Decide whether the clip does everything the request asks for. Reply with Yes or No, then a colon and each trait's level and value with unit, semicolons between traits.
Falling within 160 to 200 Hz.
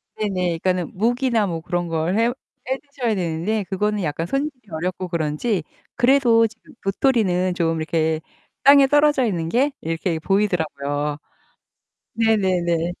Yes: medium, 185 Hz